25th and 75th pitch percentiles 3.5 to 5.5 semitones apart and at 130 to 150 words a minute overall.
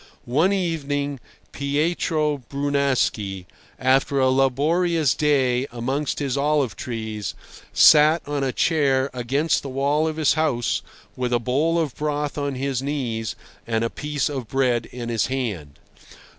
No: average, 3.1 semitones; average, 140 wpm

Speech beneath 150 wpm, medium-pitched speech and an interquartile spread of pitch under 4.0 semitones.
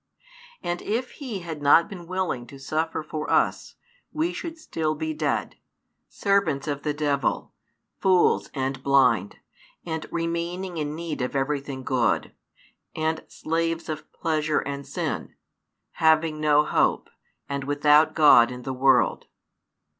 Yes: slow, 135 wpm; medium, 155 Hz; average, 3.0 semitones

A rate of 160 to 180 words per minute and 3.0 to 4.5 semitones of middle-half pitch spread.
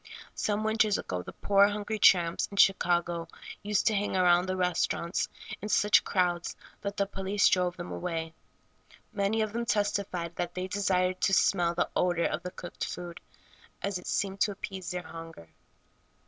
No: average, 170 wpm; narrow, 2.6 semitones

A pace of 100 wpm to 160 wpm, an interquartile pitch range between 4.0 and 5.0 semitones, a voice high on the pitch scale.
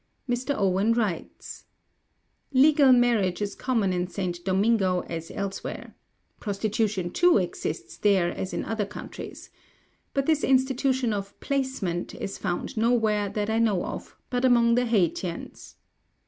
Yes: slow, 135 wpm; average, 4.6 semitones; high, 210 Hz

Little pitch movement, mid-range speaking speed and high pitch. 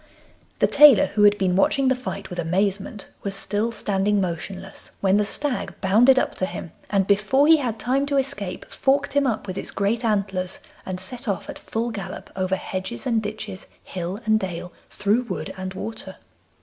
No: average, 3.9 semitones; average, 190 wpm; high, 205 Hz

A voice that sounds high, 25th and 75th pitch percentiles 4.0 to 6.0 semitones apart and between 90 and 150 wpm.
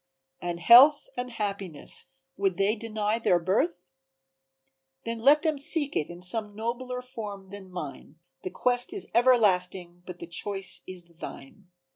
Yes: high, 205 Hz; average, 5.1 semitones; average, 145 wpm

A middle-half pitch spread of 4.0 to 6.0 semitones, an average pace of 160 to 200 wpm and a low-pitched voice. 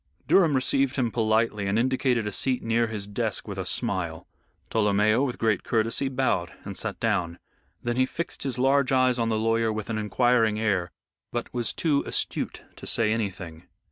No: average, 3.4 semitones; average, 180 wpm; low, 115 Hz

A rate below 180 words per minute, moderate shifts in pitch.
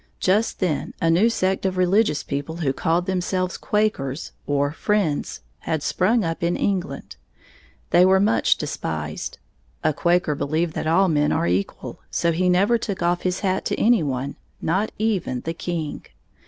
Yes: average, 165 wpm; average, 3.6 semitones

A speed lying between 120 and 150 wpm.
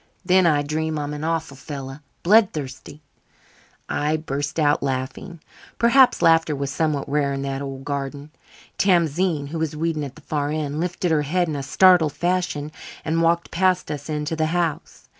No: average, 175 wpm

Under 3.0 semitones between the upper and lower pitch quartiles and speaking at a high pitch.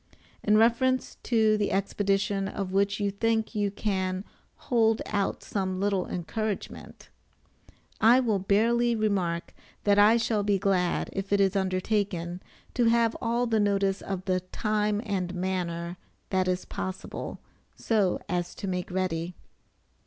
Yes: narrow, 2.6 semitones; high, 200 Hz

